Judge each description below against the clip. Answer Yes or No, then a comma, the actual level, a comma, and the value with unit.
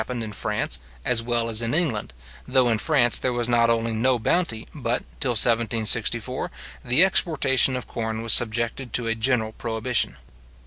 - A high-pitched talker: No, low, 120 Hz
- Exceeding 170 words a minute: Yes, average, 180 wpm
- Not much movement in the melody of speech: Yes, narrow, 2.1 semitones